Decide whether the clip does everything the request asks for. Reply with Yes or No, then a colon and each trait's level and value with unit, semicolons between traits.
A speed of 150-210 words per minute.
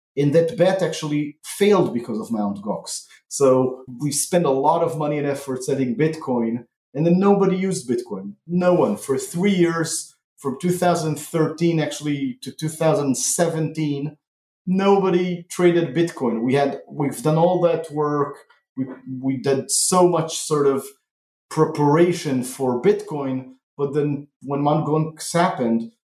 No: average, 140 wpm